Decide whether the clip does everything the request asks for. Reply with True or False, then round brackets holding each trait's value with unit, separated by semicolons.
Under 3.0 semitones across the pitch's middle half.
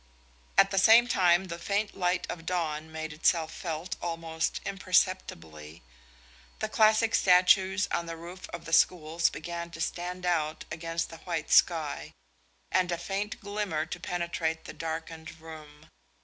True (2.5 semitones)